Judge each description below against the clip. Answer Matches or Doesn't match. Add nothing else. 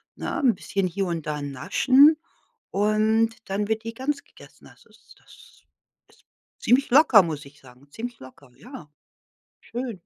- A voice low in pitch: Doesn't match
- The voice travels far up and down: Matches